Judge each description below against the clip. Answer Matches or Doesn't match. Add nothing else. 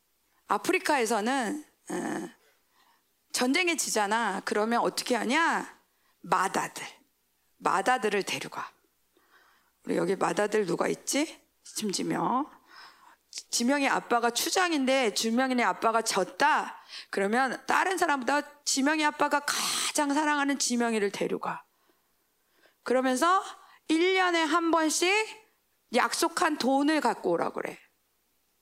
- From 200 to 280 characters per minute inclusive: Matches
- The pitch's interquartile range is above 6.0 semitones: Doesn't match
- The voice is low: Doesn't match